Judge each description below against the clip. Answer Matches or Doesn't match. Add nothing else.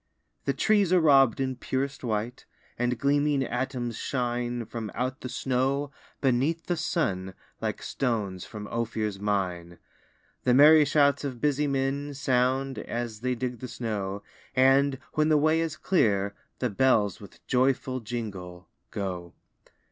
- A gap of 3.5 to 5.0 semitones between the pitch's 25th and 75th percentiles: Matches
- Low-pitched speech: Matches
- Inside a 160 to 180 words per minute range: Doesn't match